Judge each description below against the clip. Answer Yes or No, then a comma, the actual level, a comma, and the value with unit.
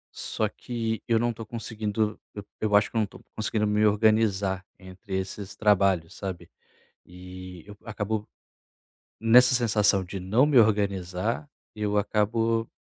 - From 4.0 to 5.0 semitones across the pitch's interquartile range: No, average, 2.7 semitones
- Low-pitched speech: Yes, low, 105 Hz